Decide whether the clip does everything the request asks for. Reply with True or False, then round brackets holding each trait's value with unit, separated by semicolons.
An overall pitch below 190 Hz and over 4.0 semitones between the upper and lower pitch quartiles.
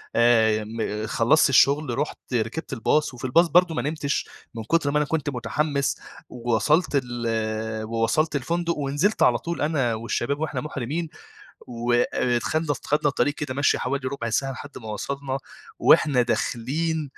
True (135 Hz; 4.4 semitones)